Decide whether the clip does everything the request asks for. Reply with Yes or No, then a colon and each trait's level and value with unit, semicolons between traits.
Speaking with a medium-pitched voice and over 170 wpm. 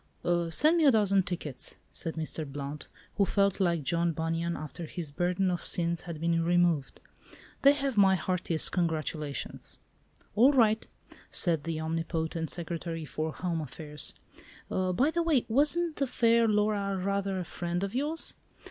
No: medium, 175 Hz; average, 150 wpm